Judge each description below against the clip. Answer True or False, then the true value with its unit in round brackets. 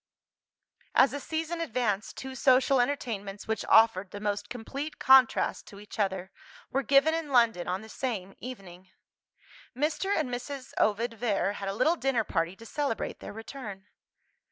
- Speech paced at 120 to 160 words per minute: True (155 wpm)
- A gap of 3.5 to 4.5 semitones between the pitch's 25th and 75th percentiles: False (5.0 semitones)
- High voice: True (235 Hz)